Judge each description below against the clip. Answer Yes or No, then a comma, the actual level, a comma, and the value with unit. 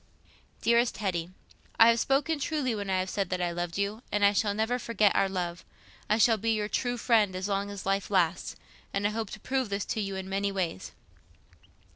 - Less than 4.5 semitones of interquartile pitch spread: Yes, average, 2.9 semitones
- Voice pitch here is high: Yes, high, 200 Hz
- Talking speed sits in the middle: No, fast, 210 wpm